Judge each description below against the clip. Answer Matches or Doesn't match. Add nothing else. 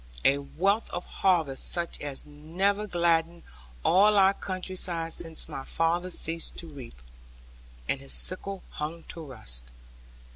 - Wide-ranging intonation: Doesn't match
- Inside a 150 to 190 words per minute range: Doesn't match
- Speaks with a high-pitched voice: Doesn't match